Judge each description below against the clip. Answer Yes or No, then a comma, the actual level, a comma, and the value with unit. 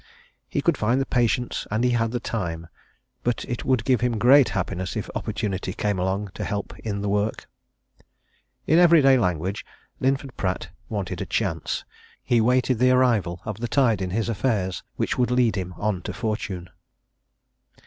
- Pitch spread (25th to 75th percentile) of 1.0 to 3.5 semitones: No, average, 4.3 semitones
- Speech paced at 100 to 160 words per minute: No, average, 170 wpm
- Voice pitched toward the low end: Yes, low, 110 Hz